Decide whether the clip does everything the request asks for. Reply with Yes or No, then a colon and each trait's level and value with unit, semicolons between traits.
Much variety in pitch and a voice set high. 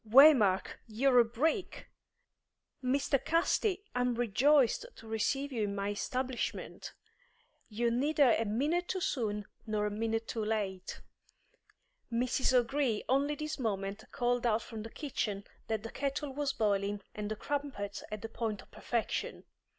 No: average, 4.4 semitones; high, 235 Hz